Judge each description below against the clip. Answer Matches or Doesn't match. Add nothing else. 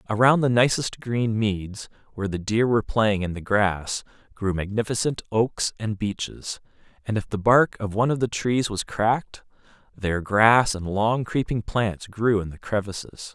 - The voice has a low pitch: Matches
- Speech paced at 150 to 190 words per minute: Matches